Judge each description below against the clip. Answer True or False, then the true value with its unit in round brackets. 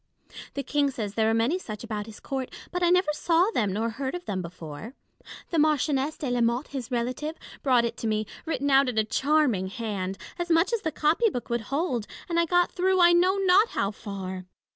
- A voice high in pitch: True (265 Hz)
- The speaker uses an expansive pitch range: True (7.2 semitones)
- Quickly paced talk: True (225 wpm)